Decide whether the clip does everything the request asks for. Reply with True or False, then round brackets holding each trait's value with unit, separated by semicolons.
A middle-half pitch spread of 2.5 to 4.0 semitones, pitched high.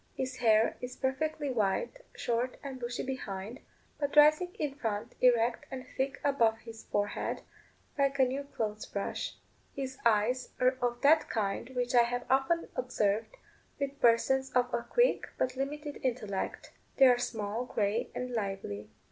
True (3.3 semitones; 250 Hz)